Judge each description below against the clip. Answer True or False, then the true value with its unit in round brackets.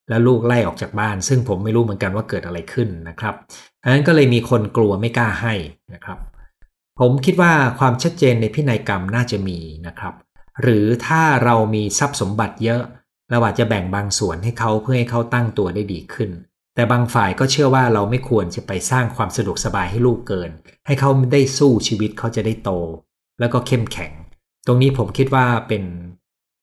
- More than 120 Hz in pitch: False (115 Hz)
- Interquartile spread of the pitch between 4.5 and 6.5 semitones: False (3.7 semitones)